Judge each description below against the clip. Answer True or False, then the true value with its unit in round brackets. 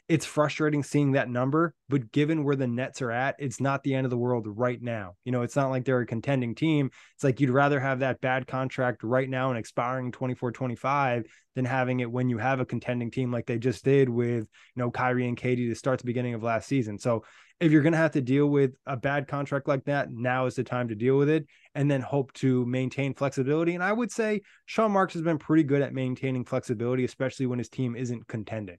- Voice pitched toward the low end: True (130 Hz)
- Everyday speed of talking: False (245 wpm)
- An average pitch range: False (2.3 semitones)